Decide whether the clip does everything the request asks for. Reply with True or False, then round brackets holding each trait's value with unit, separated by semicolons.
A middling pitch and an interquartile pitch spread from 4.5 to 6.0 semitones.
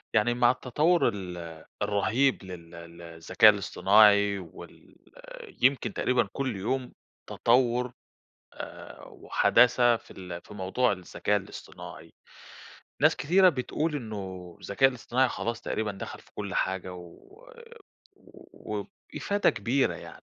False (110 Hz; 5.1 semitones)